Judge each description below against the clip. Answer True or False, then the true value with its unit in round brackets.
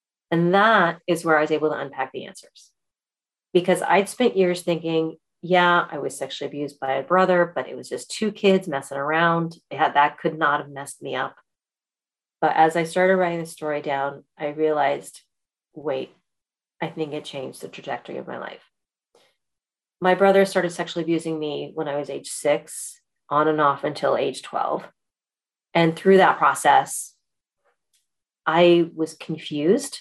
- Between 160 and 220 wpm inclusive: True (170 wpm)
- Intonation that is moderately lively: True (3.2 semitones)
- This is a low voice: False (160 Hz)